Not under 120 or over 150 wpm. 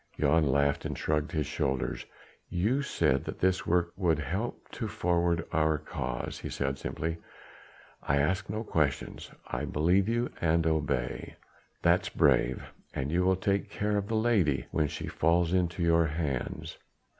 No: average, 160 wpm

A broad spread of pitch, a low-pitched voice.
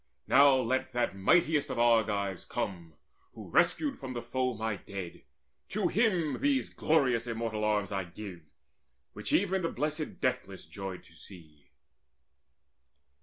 Yes: wide, 6.6 semitones; low, 115 Hz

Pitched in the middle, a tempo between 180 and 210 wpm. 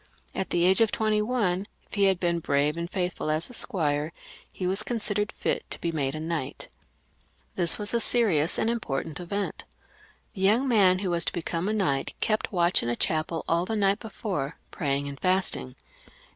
Yes: medium, 180 Hz; average, 195 wpm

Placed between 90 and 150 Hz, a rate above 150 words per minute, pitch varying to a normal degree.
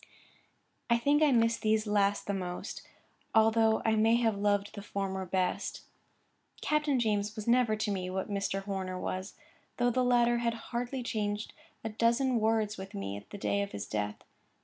No: high, 215 Hz; average, 175 wpm; average, 3.1 semitones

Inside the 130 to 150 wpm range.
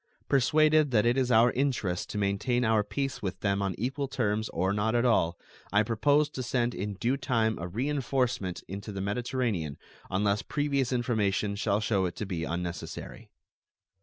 No: average, 170 wpm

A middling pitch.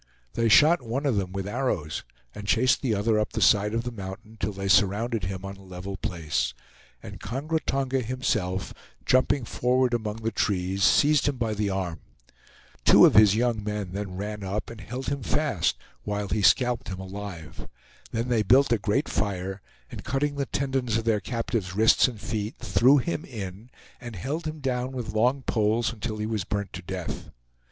No: low, 110 Hz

